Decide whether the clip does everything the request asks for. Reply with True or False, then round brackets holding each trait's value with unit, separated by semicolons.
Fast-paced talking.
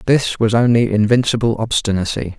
False (125 wpm)